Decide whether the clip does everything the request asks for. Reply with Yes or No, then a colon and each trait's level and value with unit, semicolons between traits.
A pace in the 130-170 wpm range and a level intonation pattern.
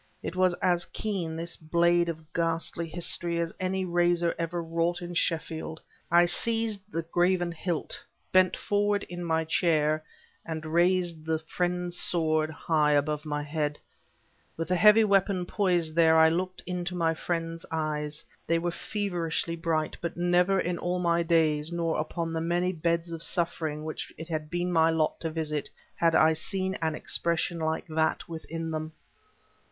Yes: average, 165 wpm; narrow, 1.6 semitones